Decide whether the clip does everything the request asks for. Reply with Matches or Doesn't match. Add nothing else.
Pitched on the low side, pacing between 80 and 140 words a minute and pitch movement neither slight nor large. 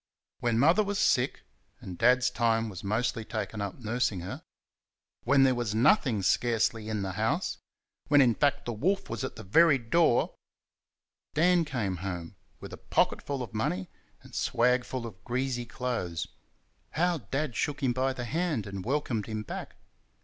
Doesn't match